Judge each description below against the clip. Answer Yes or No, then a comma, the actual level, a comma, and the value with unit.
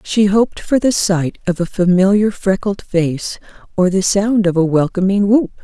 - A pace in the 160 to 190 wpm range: Yes, average, 180 wpm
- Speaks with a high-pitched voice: Yes, high, 195 Hz